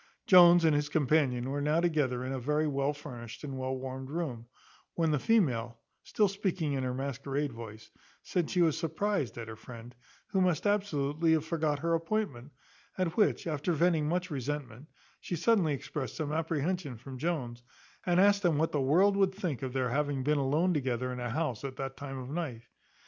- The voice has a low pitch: No, medium, 150 Hz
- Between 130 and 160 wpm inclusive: No, average, 190 wpm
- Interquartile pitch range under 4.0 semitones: No, average, 4.4 semitones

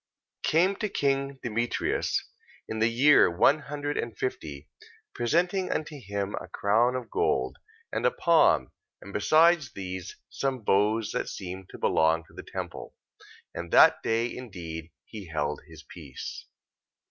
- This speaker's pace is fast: No, average, 145 wpm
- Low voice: Yes, low, 110 Hz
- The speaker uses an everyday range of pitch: No, wide, 7.3 semitones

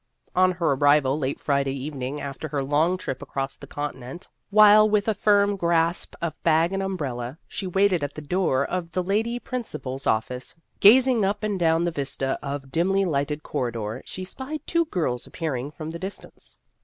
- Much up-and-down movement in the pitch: Yes, wide, 5.9 semitones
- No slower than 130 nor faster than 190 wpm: Yes, average, 180 wpm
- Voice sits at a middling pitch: Yes, medium, 165 Hz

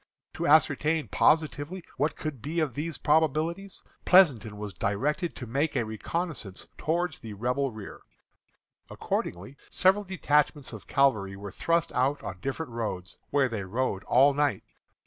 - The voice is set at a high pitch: No, medium, 140 Hz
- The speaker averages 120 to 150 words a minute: Yes, average, 145 wpm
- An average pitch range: No, wide, 6.1 semitones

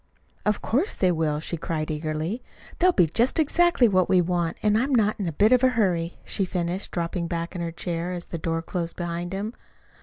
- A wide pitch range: No, average, 4.2 semitones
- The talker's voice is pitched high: No, medium, 180 Hz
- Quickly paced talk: Yes, fast, 215 wpm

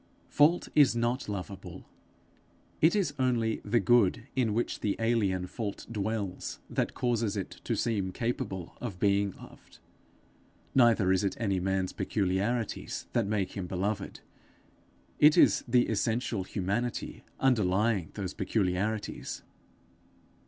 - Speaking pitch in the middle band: No, low, 105 Hz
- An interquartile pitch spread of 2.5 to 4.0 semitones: Yes, average, 3.7 semitones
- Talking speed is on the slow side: Yes, slow, 125 wpm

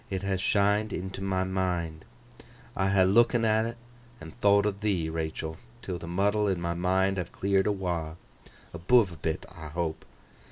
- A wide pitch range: No, average, 2.8 semitones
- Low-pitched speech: Yes, very low, 95 Hz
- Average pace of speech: Yes, average, 170 wpm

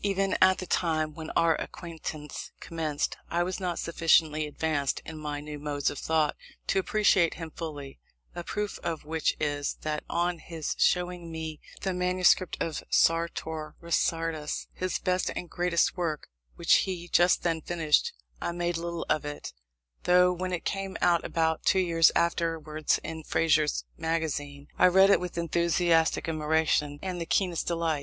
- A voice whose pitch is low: No, medium, 165 Hz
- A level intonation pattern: Yes, narrow, 2.3 semitones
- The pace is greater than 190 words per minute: No, average, 160 wpm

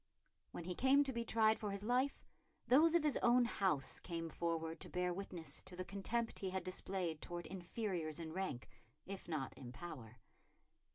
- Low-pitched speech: No, medium, 185 Hz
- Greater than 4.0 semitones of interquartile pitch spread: Yes, average, 5.2 semitones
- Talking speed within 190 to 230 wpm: No, average, 180 wpm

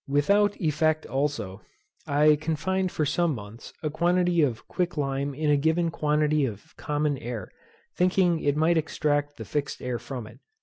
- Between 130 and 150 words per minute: No, average, 165 wpm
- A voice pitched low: No, medium, 150 Hz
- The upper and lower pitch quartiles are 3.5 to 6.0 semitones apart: No, average, 2.9 semitones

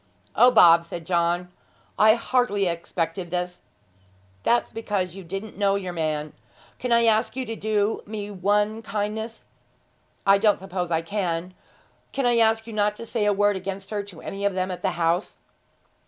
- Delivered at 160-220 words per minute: Yes, average, 170 wpm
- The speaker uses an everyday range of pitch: Yes, average, 3.5 semitones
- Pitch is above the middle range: Yes, high, 200 Hz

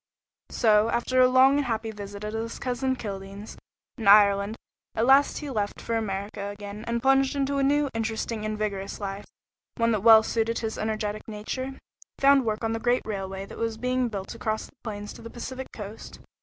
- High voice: Yes, high, 225 Hz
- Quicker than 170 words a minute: Yes, average, 195 wpm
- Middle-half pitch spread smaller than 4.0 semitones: Yes, average, 3.3 semitones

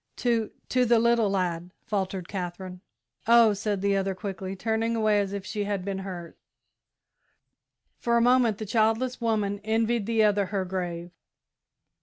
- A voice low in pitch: No, high, 205 Hz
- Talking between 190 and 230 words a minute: No, average, 155 wpm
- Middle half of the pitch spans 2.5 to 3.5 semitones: Yes, average, 3.0 semitones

